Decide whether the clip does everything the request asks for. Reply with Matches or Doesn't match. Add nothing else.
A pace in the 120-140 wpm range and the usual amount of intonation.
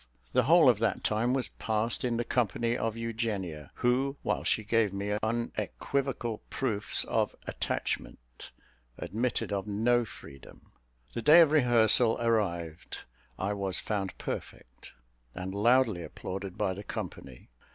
Matches